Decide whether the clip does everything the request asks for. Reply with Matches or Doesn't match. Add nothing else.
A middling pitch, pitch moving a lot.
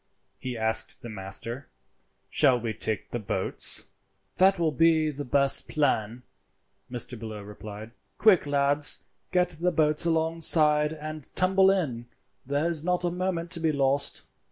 Matches